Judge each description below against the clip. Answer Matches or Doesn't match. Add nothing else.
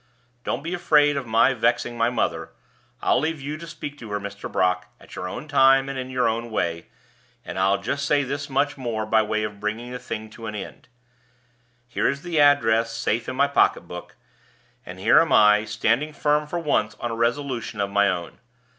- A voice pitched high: Doesn't match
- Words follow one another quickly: Matches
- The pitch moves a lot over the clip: Doesn't match